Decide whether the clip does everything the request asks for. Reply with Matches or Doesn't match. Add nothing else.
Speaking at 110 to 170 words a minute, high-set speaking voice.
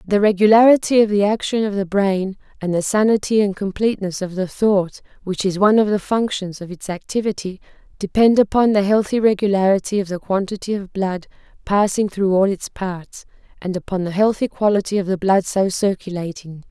Doesn't match